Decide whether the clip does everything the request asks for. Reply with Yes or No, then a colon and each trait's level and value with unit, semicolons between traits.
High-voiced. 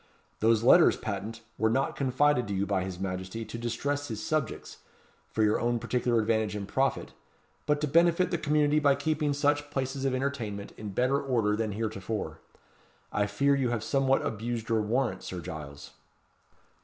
No: low, 120 Hz